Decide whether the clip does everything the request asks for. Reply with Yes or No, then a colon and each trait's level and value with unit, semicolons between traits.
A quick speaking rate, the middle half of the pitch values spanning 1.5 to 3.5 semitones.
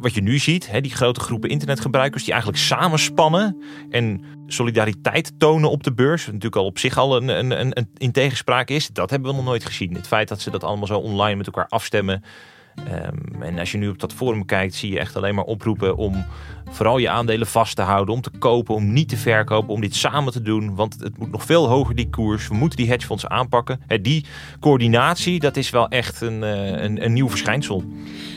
No: fast, 220 wpm; average, 4.3 semitones